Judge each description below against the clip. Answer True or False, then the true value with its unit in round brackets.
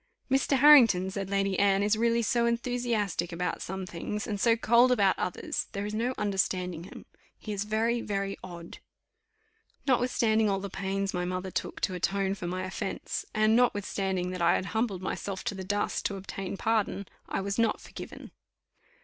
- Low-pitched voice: False (200 Hz)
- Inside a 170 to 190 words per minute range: True (175 wpm)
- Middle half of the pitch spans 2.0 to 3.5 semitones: True (3.0 semitones)